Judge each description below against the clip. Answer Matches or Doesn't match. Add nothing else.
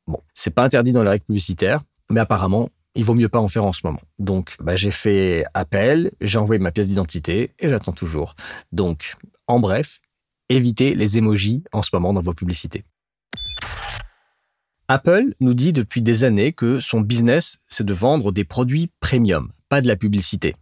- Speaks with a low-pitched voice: Matches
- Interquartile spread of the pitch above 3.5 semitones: Matches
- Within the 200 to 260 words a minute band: Doesn't match